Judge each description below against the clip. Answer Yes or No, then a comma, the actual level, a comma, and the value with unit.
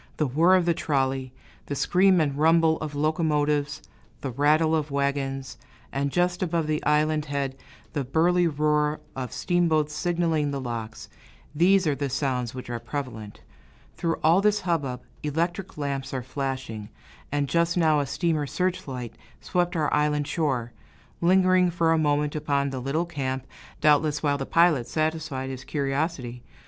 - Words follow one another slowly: No, average, 155 wpm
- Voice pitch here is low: No, medium, 150 Hz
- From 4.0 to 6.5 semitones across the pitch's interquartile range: No, average, 3.3 semitones